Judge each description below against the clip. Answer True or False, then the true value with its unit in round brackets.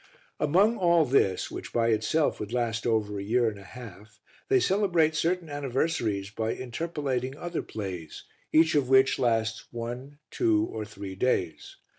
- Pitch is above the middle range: False (125 Hz)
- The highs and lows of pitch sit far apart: True (6.5 semitones)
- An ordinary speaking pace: True (155 wpm)